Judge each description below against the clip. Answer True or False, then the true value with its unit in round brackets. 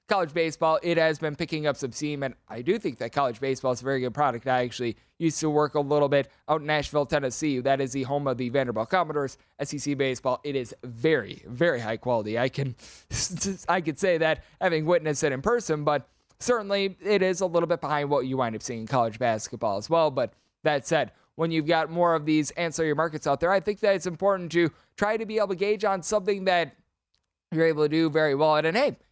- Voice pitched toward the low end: False (155 Hz)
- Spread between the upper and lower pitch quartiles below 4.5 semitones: True (4.1 semitones)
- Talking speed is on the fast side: True (235 wpm)